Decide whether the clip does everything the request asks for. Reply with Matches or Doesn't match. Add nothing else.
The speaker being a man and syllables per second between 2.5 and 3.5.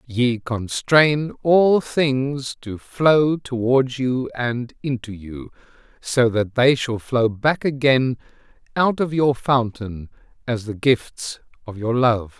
Matches